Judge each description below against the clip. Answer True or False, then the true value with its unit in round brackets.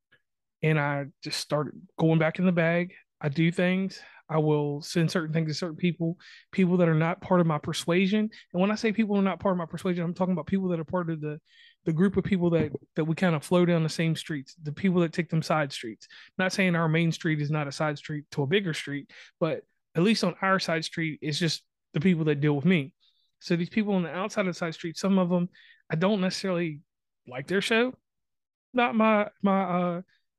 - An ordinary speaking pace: False (240 wpm)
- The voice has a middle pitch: True (175 Hz)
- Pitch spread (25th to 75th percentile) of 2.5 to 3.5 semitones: True (3.0 semitones)